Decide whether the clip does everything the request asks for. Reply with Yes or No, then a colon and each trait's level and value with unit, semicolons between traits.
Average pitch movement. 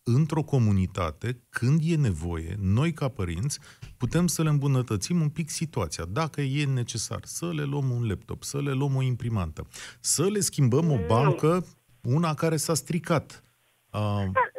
No: wide, 6.3 semitones